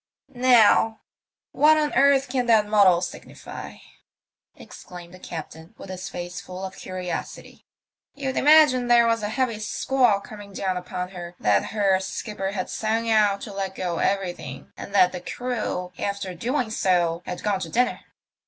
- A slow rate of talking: No, average, 160 wpm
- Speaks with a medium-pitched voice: No, high, 200 Hz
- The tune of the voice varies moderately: Yes, average, 4.7 semitones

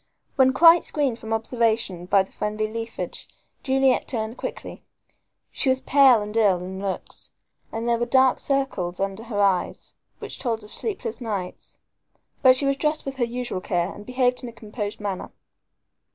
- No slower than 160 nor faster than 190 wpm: Yes, average, 170 wpm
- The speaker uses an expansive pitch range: No, average, 4.2 semitones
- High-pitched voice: Yes, high, 230 Hz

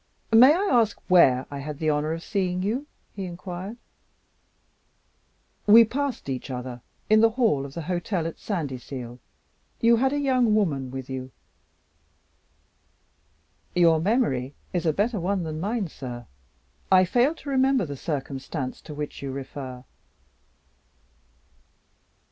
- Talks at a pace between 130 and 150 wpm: Yes, slow, 135 wpm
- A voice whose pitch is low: No, medium, 175 Hz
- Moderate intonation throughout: No, wide, 8.2 semitones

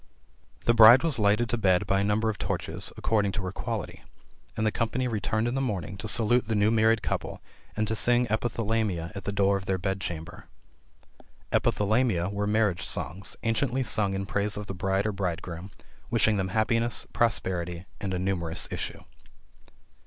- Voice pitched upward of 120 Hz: No, low, 105 Hz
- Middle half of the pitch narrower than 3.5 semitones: Yes, average, 2.8 semitones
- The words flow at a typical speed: Yes, average, 180 wpm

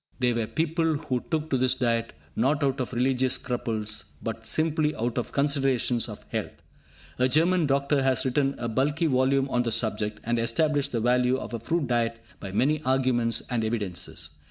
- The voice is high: No, low, 130 Hz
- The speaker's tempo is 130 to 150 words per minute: No, average, 180 wpm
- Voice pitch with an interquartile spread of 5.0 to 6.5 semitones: No, average, 3.3 semitones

